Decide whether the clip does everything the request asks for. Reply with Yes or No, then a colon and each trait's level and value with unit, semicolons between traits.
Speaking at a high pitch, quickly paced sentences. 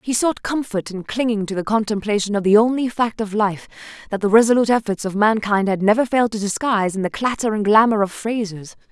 Yes: high, 215 Hz; fast, 215 wpm